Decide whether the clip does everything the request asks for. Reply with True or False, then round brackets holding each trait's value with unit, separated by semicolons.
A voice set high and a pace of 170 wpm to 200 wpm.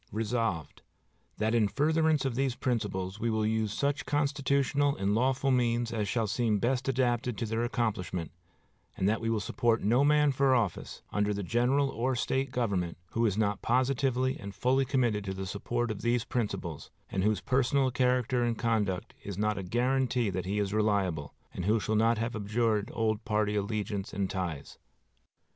False (115 Hz; 180 wpm)